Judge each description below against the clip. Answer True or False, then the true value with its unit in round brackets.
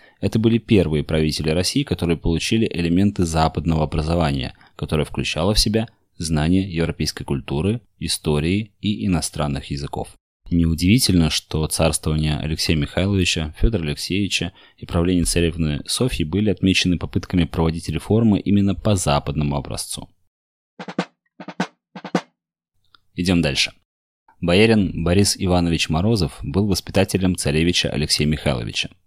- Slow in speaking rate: True (105 wpm)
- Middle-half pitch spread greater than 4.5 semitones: False (4.0 semitones)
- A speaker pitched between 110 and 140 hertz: False (85 Hz)